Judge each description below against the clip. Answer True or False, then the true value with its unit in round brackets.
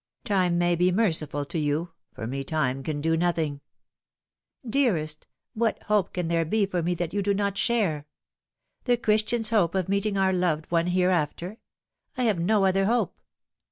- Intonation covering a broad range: False (4.1 semitones)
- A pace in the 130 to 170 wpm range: False (180 wpm)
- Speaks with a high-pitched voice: False (180 Hz)